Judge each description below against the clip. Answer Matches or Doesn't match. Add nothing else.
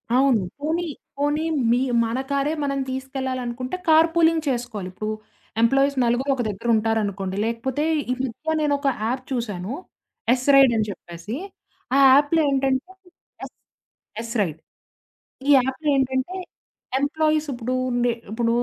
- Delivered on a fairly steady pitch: Doesn't match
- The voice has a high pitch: Matches